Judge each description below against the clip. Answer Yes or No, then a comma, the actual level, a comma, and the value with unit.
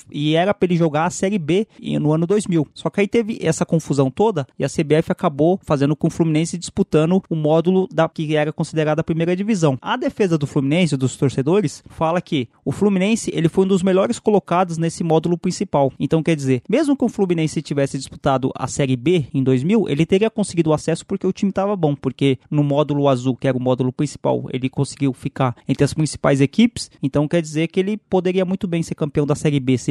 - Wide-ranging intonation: No, average, 4.7 semitones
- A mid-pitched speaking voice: Yes, medium, 160 Hz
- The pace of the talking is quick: Yes, fast, 220 wpm